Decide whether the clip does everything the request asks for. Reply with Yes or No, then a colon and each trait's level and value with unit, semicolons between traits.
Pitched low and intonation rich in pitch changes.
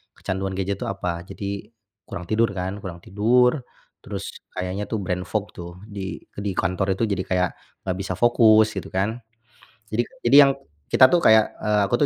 No: low, 100 Hz; average, 2.8 semitones